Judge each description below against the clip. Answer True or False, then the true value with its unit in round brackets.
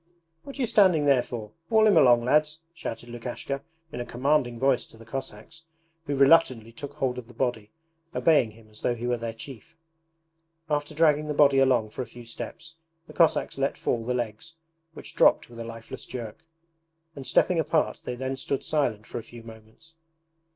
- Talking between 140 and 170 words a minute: False (195 wpm)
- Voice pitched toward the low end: True (130 Hz)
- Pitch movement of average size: True (4.6 semitones)